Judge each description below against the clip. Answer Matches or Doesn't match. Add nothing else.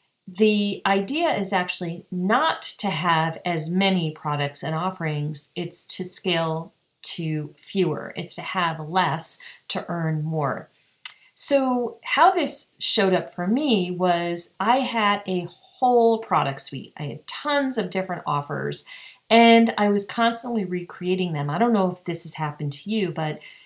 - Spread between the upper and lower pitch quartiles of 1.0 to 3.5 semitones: Doesn't match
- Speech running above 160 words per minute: Doesn't match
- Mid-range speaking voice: Matches